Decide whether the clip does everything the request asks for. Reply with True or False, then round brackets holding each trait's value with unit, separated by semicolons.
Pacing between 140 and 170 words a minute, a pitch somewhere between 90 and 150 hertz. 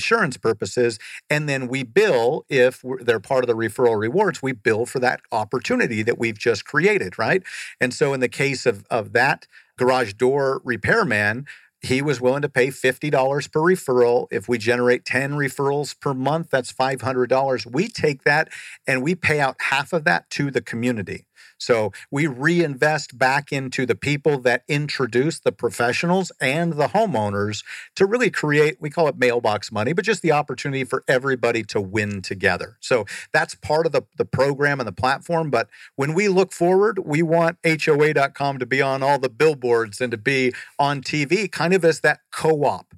False (180 wpm; 135 Hz)